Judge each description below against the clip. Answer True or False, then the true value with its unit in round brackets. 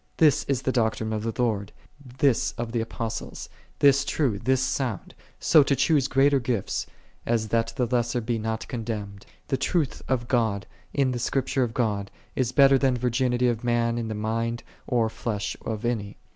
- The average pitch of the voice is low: True (120 Hz)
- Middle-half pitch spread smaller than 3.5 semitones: True (2.8 semitones)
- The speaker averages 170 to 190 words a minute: True (185 wpm)